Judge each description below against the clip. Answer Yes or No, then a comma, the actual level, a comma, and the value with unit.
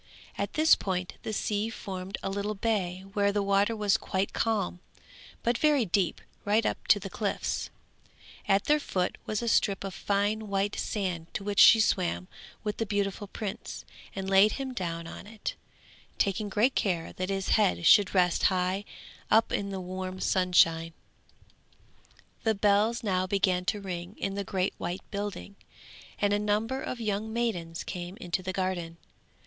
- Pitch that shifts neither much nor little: No, narrow, 2.3 semitones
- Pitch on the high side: Yes, high, 200 Hz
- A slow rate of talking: No, average, 165 wpm